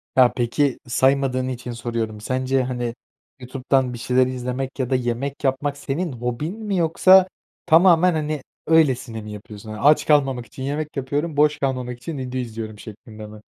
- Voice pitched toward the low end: Yes, low, 130 Hz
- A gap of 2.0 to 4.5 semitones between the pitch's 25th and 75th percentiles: Yes, average, 3.2 semitones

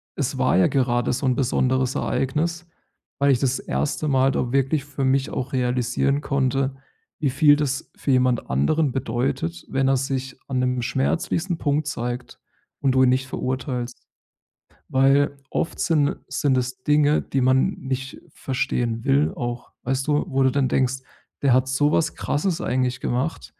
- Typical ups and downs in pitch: No, narrow, 2.0 semitones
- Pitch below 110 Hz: No, low, 130 Hz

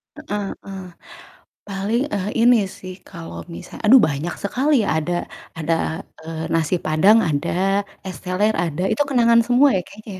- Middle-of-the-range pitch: No, high, 195 Hz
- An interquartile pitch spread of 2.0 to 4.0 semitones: No, average, 4.4 semitones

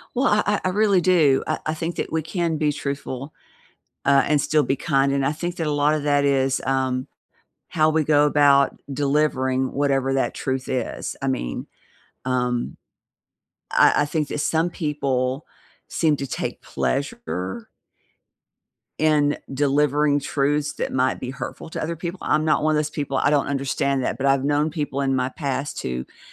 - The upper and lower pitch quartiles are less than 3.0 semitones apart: Yes, narrow, 2.4 semitones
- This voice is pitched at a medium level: Yes, medium, 145 Hz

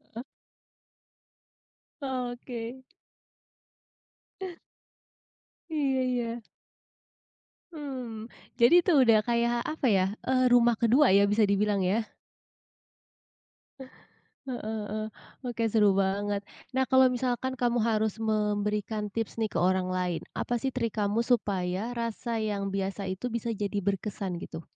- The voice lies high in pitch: Yes, high, 225 Hz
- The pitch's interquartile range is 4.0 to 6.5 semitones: No, average, 3.1 semitones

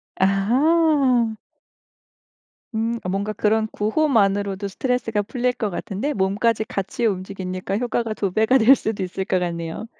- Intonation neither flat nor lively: Yes, average, 3.5 semitones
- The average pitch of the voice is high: Yes, high, 215 Hz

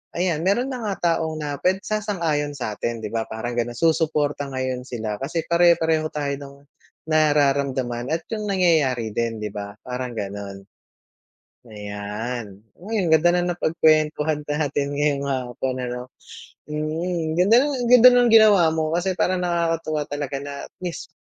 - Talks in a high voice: No, medium, 150 Hz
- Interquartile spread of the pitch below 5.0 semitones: No, wide, 5.4 semitones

